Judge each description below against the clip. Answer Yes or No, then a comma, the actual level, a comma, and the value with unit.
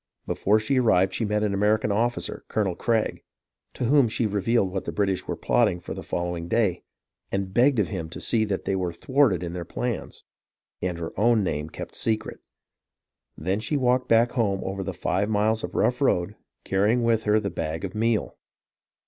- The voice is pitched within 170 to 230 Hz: No, low, 105 Hz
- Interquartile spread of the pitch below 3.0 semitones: No, average, 3.8 semitones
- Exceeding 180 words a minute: Yes, average, 190 wpm